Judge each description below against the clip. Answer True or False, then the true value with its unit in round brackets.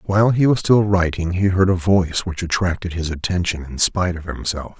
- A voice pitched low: True (90 Hz)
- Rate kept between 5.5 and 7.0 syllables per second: True (5.6 syllables/s)